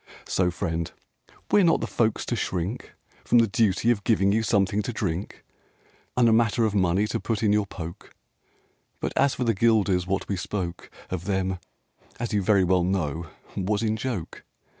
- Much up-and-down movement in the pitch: No, average, 3.5 semitones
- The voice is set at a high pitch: No, low, 100 Hz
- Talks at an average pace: Yes, average, 190 wpm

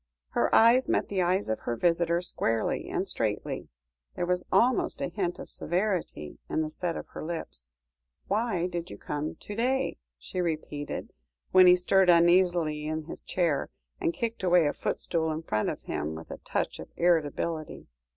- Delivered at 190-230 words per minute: No, average, 175 wpm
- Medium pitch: Yes, medium, 175 Hz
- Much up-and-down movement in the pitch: No, average, 3.2 semitones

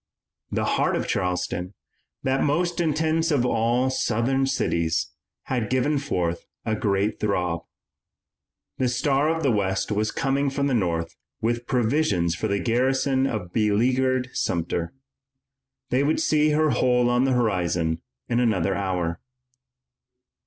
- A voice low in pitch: Yes, low, 120 Hz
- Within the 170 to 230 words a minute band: No, slow, 135 wpm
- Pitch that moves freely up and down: Yes, wide, 6.1 semitones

